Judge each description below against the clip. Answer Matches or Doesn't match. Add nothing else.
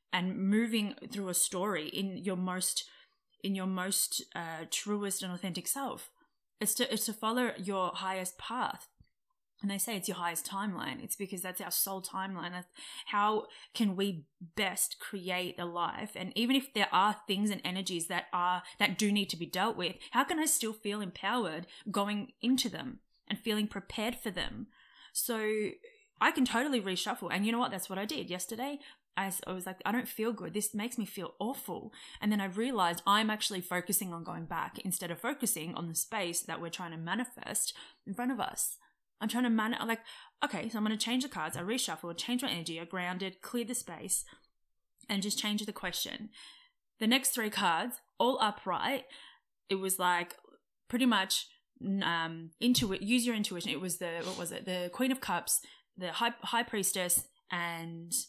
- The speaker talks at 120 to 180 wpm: Doesn't match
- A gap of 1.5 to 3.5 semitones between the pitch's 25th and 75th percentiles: Doesn't match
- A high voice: Matches